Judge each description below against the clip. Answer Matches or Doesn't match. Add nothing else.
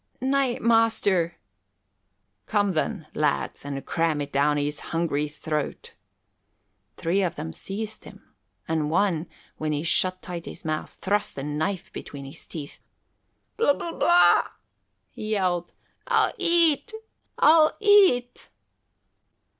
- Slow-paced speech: Matches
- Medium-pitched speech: Matches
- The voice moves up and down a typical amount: Doesn't match